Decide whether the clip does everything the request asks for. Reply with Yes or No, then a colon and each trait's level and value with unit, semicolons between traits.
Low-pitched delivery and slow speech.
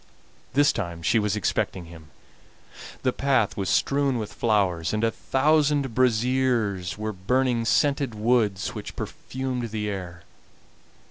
Yes: low, 115 Hz; slow, 130 wpm